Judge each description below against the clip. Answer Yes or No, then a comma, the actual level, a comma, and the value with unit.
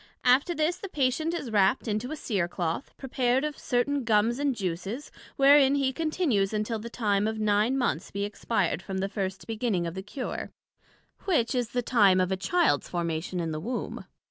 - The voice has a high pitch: Yes, high, 230 Hz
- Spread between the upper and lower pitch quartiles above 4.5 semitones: Yes, wide, 5.6 semitones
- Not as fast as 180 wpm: No, average, 190 wpm